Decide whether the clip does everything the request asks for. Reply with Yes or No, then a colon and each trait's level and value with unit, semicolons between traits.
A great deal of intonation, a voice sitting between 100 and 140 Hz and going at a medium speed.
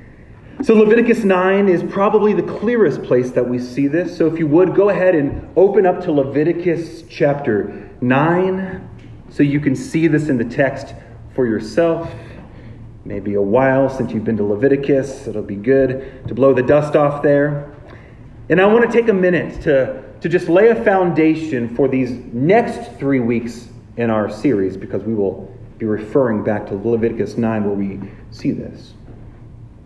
Yes: wide, 6.4 semitones; low, 135 Hz; average, 175 wpm